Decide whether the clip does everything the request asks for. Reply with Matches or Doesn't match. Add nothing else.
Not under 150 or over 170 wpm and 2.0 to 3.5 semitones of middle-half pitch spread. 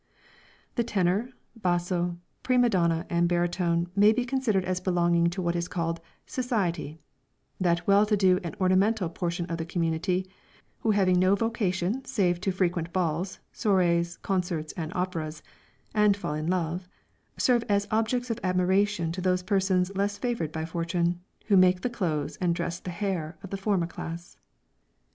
Matches